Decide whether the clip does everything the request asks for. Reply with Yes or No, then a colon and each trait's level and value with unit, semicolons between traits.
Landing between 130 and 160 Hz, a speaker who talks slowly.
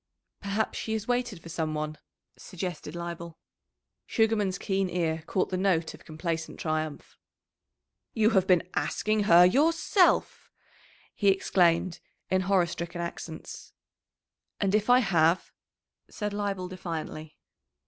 No: medium, 185 Hz; slow, 125 wpm